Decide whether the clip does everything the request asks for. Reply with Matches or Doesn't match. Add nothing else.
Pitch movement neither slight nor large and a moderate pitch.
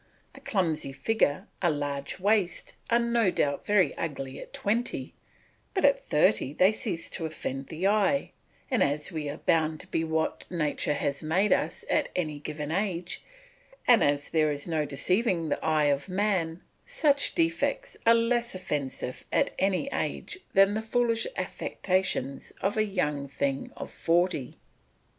Doesn't match